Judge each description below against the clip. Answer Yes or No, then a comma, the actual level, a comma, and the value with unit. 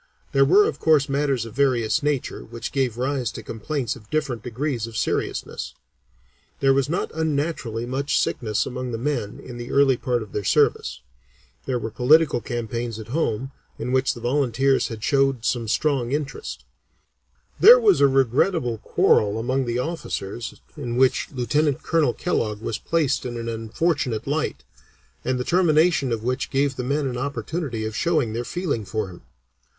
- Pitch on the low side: Yes, low, 130 Hz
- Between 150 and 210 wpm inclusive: Yes, average, 170 wpm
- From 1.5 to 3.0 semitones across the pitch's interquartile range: No, average, 3.8 semitones